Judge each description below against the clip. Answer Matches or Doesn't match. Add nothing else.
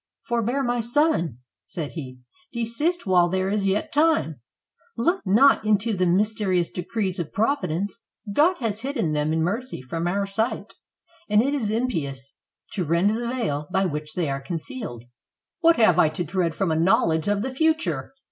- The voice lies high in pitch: Matches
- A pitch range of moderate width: Doesn't match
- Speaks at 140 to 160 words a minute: Doesn't match